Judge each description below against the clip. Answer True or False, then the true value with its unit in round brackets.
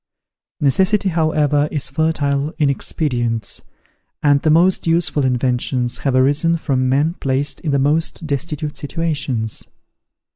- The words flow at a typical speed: False (120 wpm)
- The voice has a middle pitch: True (145 Hz)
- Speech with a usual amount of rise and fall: True (3.1 semitones)